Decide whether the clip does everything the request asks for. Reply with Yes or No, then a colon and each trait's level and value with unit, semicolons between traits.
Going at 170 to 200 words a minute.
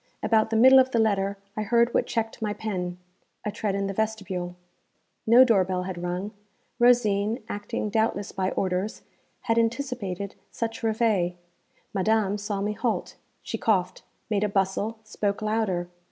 No: average, 155 wpm